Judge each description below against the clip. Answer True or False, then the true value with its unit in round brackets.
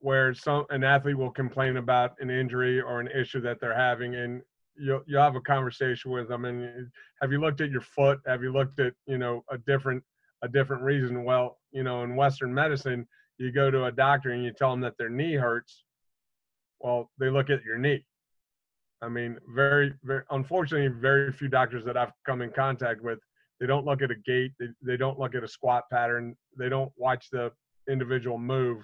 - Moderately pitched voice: False (130 Hz)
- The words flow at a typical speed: False (210 wpm)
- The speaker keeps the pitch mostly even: True (1.9 semitones)